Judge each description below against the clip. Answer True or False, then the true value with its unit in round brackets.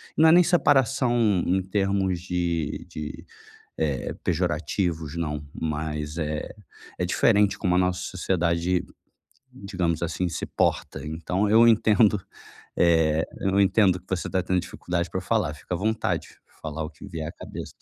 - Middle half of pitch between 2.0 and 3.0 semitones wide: False (3.4 semitones)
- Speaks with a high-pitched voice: False (90 Hz)